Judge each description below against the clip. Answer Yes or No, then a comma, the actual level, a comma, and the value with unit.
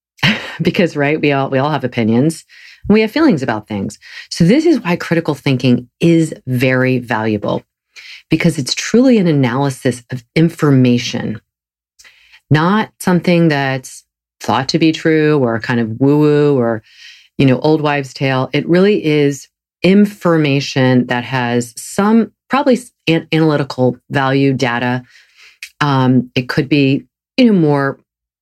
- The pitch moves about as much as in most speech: Yes, average, 4.6 semitones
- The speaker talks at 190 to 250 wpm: No, slow, 135 wpm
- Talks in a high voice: No, medium, 140 Hz